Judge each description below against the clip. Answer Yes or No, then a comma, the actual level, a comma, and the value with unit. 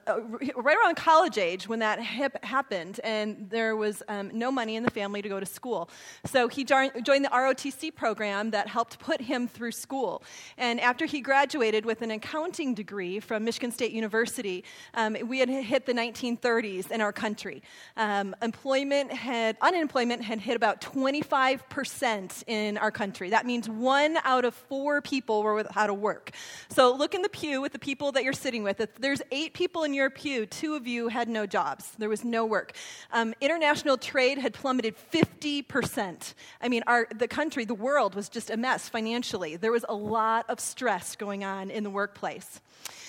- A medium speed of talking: Yes, average, 190 wpm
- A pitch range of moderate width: Yes, average, 3.8 semitones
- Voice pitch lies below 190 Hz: No, high, 240 Hz